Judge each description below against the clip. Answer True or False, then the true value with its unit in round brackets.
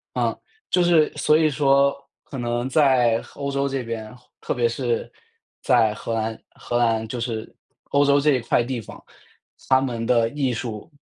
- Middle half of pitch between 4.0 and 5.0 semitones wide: False (3.3 semitones)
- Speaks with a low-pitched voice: True (125 Hz)